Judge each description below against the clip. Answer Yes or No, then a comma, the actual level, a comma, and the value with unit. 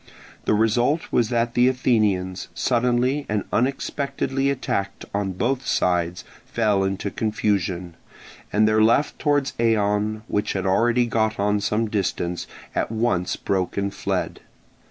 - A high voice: No, low, 110 Hz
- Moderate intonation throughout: Yes, average, 3.5 semitones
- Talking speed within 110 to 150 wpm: Yes, slow, 135 wpm